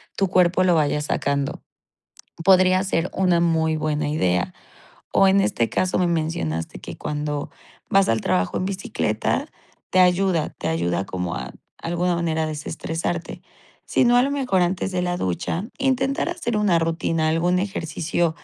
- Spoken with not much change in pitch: No, average, 3.7 semitones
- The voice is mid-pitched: Yes, medium, 170 Hz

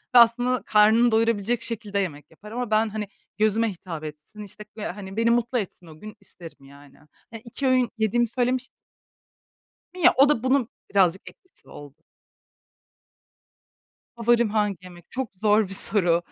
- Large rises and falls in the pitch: No, average, 3.8 semitones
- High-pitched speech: Yes, high, 215 Hz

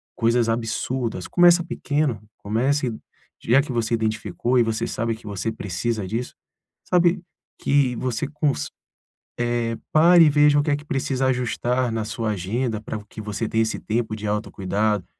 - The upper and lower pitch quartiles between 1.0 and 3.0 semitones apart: No, average, 3.7 semitones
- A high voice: No, low, 115 Hz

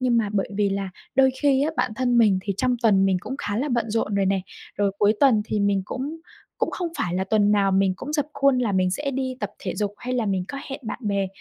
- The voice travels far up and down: No, average, 4.7 semitones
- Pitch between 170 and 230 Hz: Yes, high, 215 Hz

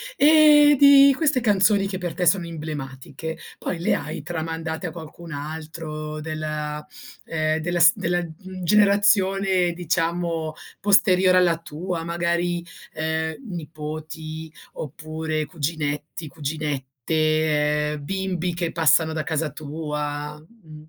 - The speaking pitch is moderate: Yes, medium, 160 Hz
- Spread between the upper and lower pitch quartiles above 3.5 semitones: No, average, 2.7 semitones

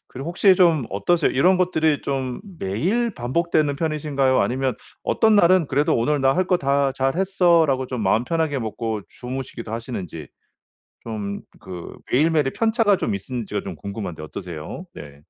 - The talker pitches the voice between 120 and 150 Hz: Yes, low, 135 Hz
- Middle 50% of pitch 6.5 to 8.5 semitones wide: Yes, wide, 6.8 semitones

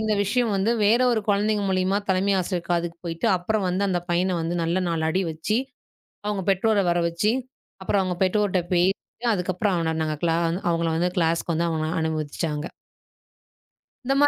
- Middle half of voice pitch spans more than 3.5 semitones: No, average, 3.2 semitones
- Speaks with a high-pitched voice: No, medium, 180 Hz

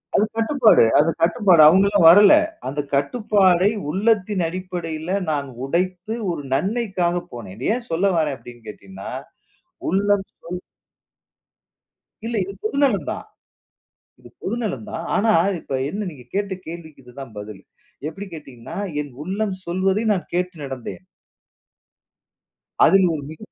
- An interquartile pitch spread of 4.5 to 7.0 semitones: Yes, average, 5.3 semitones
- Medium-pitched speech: Yes, medium, 180 Hz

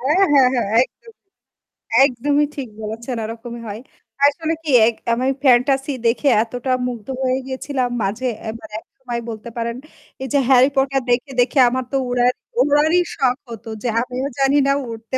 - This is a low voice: No, very high, 255 Hz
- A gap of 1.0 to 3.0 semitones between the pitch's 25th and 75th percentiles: Yes, average, 2.7 semitones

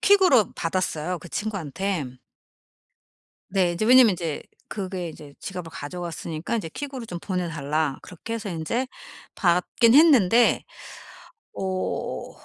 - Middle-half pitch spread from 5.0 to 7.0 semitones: Yes, wide, 5.4 semitones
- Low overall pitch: No, medium, 185 Hz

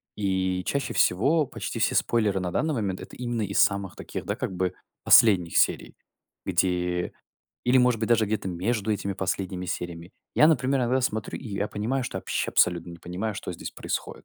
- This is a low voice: Yes, low, 100 Hz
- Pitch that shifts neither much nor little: Yes, average, 4.7 semitones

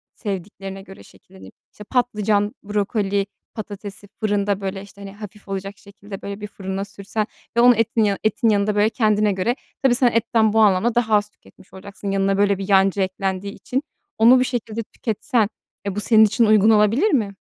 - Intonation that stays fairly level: Yes, narrow, 1.9 semitones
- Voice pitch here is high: Yes, high, 205 Hz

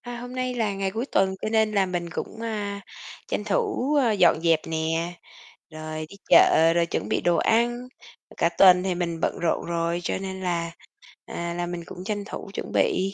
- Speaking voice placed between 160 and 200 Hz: Yes, high, 190 Hz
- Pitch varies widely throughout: No, average, 4.4 semitones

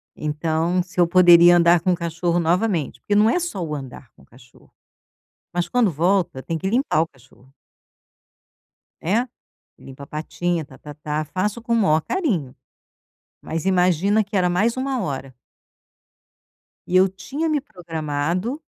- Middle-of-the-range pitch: Yes, medium, 175 Hz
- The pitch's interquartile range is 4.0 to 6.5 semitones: Yes, average, 4.6 semitones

